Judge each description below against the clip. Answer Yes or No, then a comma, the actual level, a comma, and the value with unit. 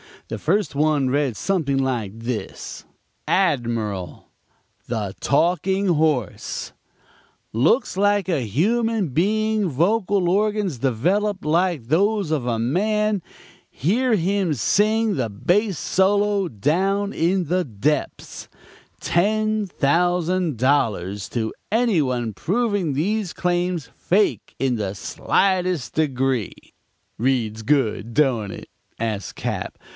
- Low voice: No, medium, 165 Hz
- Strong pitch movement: Yes, wide, 8.1 semitones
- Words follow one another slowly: Yes, slow, 110 wpm